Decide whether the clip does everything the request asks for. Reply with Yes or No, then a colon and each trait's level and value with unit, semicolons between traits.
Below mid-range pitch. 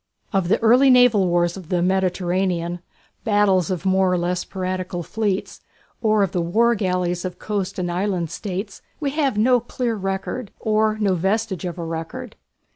No: high, 190 Hz